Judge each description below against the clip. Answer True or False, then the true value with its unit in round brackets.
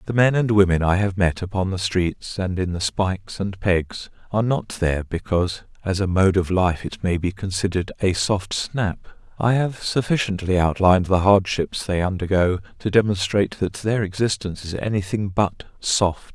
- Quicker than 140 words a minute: True (180 wpm)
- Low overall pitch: True (95 Hz)